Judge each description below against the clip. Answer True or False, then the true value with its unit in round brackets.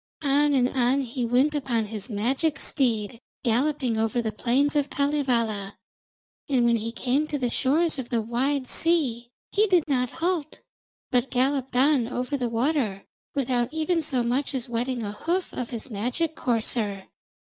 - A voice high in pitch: True (255 Hz)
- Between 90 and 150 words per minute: False (165 wpm)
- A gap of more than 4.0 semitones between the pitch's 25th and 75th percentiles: False (3.6 semitones)